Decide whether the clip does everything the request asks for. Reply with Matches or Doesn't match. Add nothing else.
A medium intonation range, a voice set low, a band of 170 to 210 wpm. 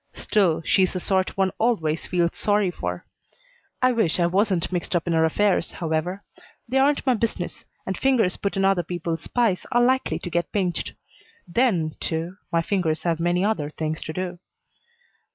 Doesn't match